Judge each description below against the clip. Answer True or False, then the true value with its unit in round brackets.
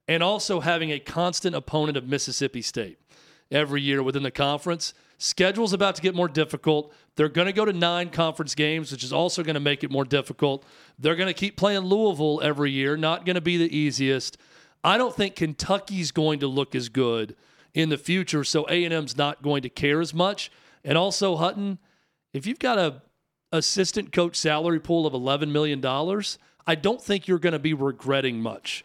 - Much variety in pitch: False (3.8 semitones)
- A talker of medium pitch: True (155 Hz)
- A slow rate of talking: False (200 wpm)